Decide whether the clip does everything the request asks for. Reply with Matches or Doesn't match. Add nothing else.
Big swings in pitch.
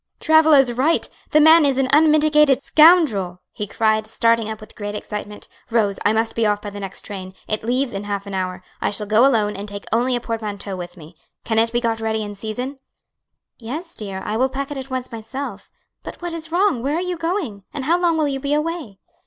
Matches